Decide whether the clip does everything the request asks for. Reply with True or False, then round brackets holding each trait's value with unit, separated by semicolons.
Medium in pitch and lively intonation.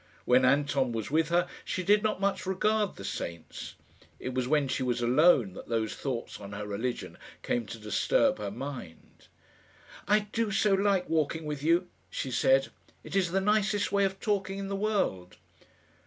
True (160 Hz; 8.5 semitones)